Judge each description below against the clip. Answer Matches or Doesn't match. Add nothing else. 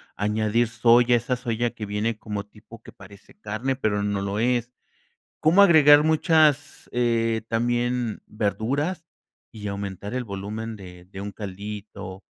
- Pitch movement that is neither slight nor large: Matches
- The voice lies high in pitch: Doesn't match